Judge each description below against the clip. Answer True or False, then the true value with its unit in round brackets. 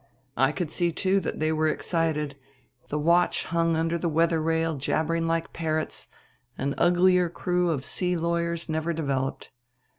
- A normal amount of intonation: False (1.5 semitones)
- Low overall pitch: False (165 Hz)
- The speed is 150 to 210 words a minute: True (155 wpm)